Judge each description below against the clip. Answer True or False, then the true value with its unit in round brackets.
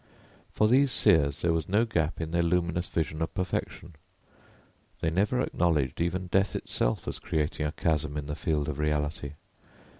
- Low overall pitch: True (80 Hz)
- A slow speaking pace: False (170 wpm)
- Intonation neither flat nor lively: True (3.1 semitones)